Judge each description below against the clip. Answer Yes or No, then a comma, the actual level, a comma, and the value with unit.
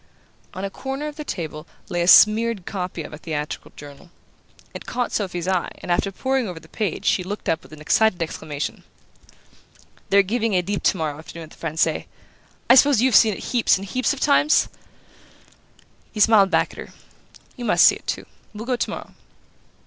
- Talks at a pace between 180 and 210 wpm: Yes, average, 185 wpm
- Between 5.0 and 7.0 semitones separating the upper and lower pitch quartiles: Yes, wide, 5.6 semitones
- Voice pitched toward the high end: Yes, high, 195 Hz